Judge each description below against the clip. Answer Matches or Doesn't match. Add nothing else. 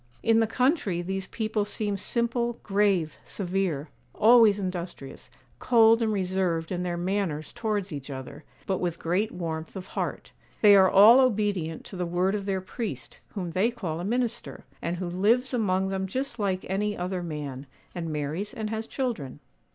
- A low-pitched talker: Doesn't match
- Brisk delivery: Doesn't match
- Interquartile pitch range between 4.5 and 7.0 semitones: Doesn't match